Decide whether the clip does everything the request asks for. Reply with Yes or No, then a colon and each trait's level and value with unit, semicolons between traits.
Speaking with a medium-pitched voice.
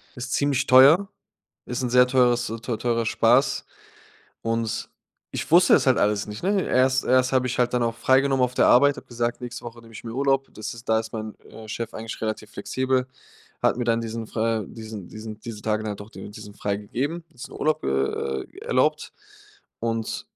No: low, 115 Hz